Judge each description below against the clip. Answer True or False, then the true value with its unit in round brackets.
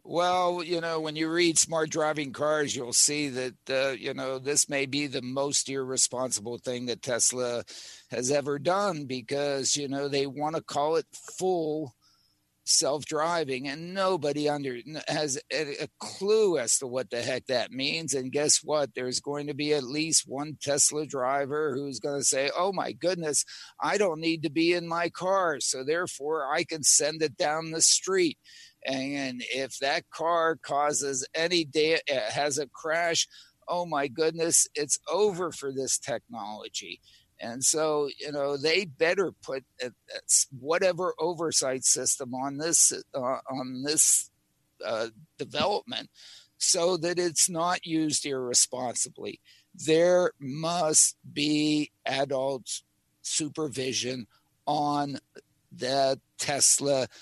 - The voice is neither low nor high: True (150 Hz)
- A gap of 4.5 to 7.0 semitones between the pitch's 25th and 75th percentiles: False (3.4 semitones)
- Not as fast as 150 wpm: True (140 wpm)